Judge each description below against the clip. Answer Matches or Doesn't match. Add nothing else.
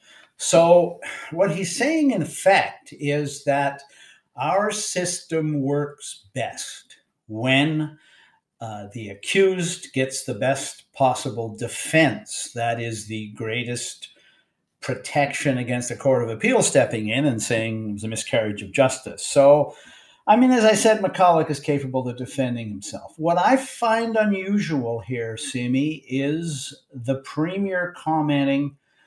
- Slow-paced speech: Matches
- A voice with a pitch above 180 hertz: Doesn't match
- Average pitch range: Doesn't match